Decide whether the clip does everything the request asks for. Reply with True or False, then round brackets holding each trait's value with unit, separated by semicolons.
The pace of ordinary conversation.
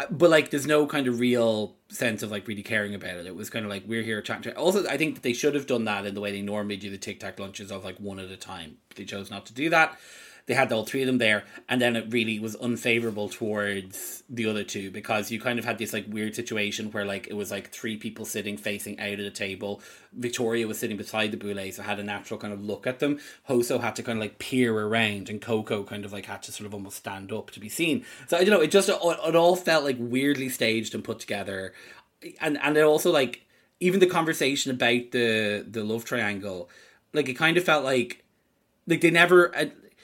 False (255 wpm)